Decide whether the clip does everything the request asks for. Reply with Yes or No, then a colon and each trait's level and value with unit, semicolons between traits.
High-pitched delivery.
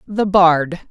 No: medium, 180 Hz